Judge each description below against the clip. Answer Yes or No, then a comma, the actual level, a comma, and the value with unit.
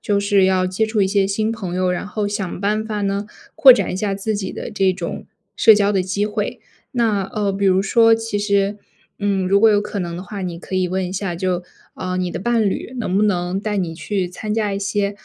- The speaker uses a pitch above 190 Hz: Yes, high, 200 Hz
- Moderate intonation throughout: No, narrow, 2.0 semitones